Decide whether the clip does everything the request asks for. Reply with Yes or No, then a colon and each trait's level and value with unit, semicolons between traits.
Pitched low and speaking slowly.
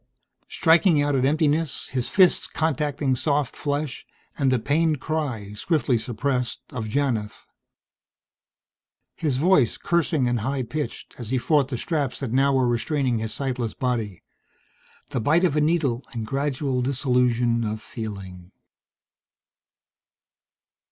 Yes: low, 130 Hz; slow, 130 wpm